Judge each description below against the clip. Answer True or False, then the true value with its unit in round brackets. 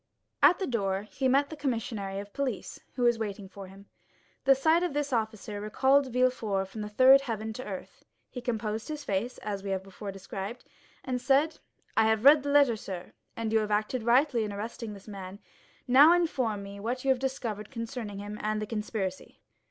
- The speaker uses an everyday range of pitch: True (4.3 semitones)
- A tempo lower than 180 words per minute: False (200 wpm)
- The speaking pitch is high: True (225 Hz)